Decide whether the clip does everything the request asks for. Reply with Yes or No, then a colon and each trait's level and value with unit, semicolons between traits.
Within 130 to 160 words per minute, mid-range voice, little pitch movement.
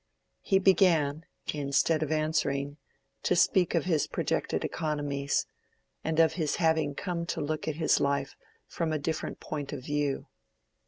Yes: average, 150 wpm; medium, 155 Hz; narrow, 2.2 semitones